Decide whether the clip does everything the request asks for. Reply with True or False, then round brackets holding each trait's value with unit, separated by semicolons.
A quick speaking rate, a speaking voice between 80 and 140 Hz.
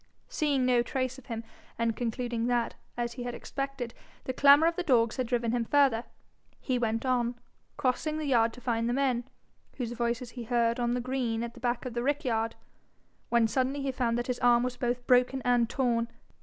False (210 wpm; 245 Hz)